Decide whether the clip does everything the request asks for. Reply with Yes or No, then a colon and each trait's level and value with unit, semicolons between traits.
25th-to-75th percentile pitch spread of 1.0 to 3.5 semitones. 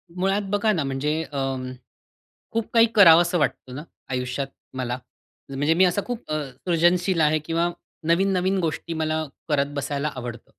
No: average, 4.5 semitones